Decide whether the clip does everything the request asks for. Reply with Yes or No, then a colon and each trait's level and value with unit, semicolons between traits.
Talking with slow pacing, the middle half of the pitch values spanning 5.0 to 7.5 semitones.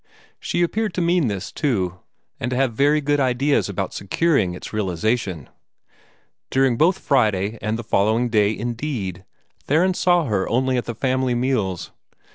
No: average, 155 wpm; wide, 5.5 semitones